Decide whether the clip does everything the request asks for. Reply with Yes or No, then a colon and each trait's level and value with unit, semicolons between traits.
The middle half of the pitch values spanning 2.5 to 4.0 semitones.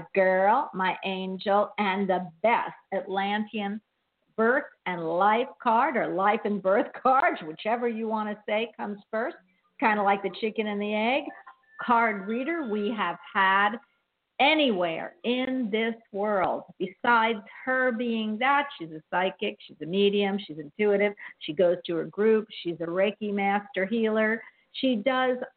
Yes: average, 3.5 semitones